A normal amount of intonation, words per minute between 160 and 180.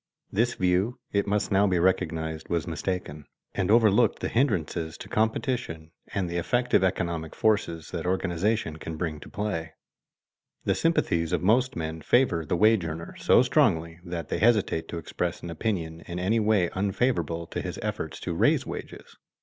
Yes: average, 4.5 semitones; average, 165 wpm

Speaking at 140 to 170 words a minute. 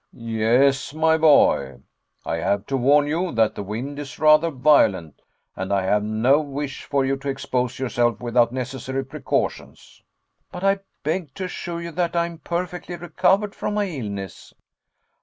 Yes: average, 160 wpm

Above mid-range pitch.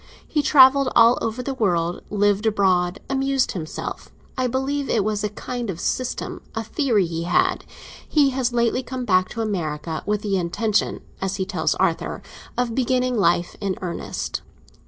Yes: high, 220 Hz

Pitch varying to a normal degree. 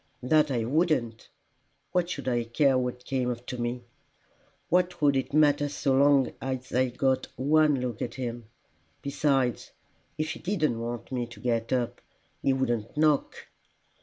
Yes: average, 3.3 semitones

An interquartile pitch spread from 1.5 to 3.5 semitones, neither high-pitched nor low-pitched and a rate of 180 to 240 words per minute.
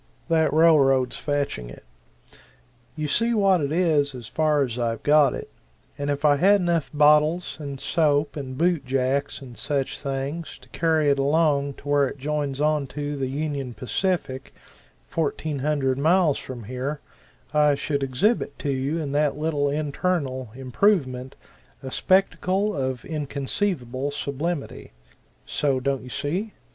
No: average, 2.7 semitones; medium, 145 Hz; average, 145 wpm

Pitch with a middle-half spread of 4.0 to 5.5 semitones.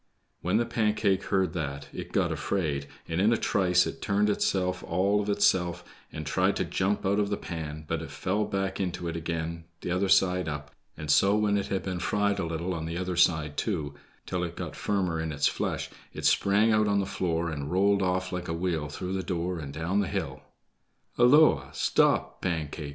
No: average, 3.4 semitones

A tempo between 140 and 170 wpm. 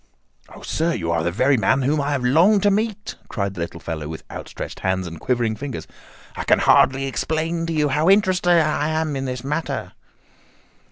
No: average, 200 wpm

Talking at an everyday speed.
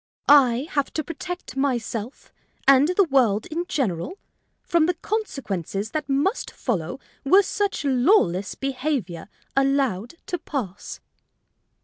No: slow, 115 wpm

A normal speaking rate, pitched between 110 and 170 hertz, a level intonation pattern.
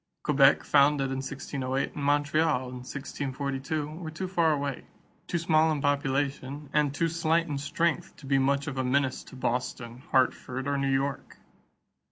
Yes: average, 165 wpm; medium, 140 Hz; narrow, 2.1 semitones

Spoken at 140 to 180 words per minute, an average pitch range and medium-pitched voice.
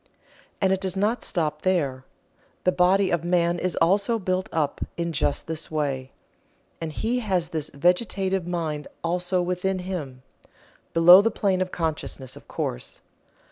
Yes: average, 150 wpm; average, 3.1 semitones; medium, 180 Hz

